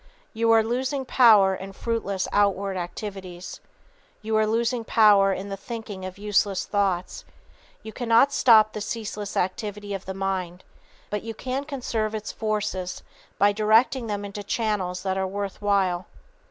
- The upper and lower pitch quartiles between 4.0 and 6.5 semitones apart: No, narrow, 2.6 semitones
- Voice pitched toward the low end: No, high, 205 Hz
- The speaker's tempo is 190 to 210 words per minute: No, average, 155 wpm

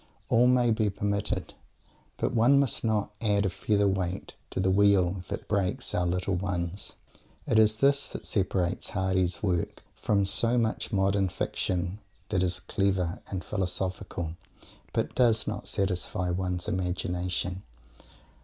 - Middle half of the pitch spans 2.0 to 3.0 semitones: Yes, narrow, 2.6 semitones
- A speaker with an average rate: Yes, average, 145 wpm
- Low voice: Yes, very low, 95 Hz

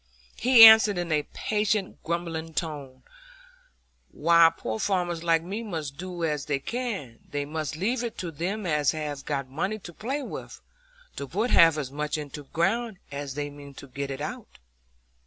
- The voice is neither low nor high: Yes, medium, 165 Hz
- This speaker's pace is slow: No, average, 180 wpm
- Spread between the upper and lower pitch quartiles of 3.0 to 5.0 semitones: No, wide, 5.4 semitones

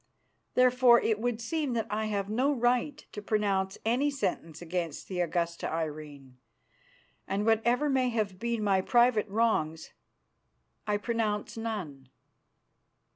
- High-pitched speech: Yes, high, 215 Hz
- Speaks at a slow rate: Yes, slow, 130 wpm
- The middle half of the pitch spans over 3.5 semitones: Yes, average, 4.6 semitones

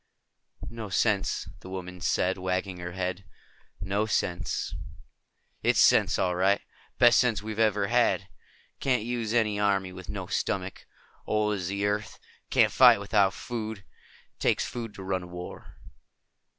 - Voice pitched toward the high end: No, low, 100 Hz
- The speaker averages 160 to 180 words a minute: No, average, 145 wpm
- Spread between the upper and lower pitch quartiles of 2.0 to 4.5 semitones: Yes, average, 2.7 semitones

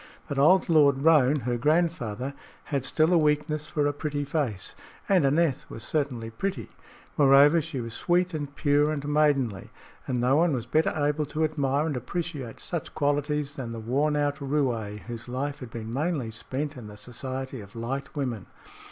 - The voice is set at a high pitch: No, medium, 140 Hz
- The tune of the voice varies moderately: Yes, average, 3.4 semitones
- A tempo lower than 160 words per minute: No, average, 180 wpm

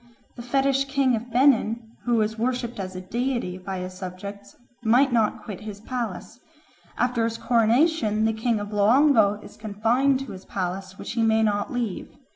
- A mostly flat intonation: No, average, 3.4 semitones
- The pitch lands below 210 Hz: No, high, 225 Hz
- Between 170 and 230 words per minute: Yes, average, 175 wpm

